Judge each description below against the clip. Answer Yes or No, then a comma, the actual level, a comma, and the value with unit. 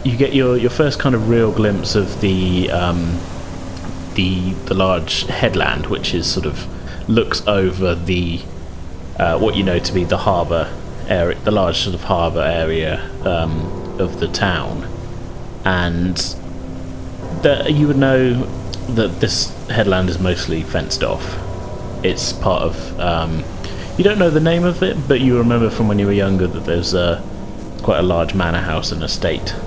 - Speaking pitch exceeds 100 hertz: No, very low, 95 Hz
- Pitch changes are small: No, average, 4.4 semitones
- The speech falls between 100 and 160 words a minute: No, average, 170 wpm